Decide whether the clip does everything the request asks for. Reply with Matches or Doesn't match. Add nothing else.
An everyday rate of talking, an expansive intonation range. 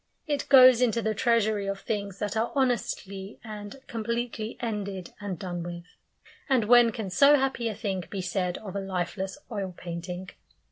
Doesn't match